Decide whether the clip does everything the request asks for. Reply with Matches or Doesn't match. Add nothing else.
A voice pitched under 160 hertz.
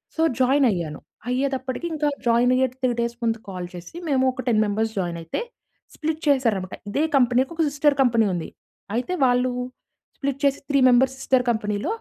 Doesn't match